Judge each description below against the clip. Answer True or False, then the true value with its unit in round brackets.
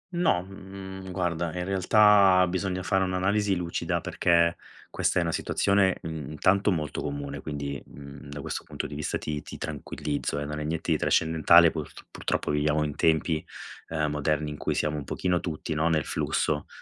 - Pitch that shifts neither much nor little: True (3.6 semitones)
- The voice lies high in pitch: False (80 Hz)